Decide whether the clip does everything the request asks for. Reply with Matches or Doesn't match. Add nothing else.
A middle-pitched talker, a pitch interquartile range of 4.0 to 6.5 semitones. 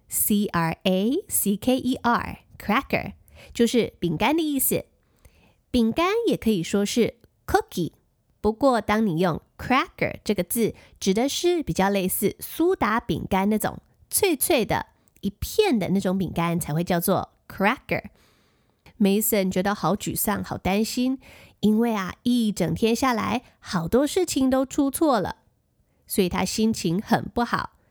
Doesn't match